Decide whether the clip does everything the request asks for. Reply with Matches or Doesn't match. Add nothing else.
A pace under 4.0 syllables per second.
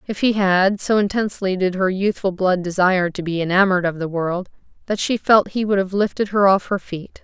Doesn't match